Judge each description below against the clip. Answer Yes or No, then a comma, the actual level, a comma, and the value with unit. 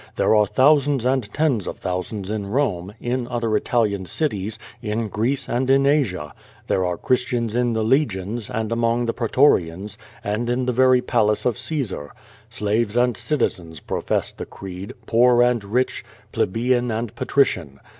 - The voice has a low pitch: Yes, low, 115 Hz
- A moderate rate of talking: Yes, average, 155 wpm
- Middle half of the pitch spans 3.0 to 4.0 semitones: Yes, average, 3.6 semitones